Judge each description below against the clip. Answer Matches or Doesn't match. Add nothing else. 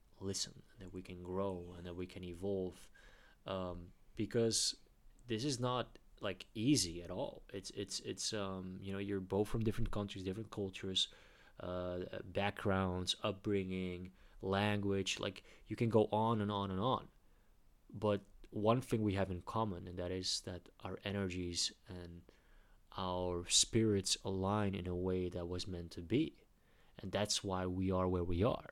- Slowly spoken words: Doesn't match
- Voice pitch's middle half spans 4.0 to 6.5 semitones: Doesn't match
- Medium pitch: Doesn't match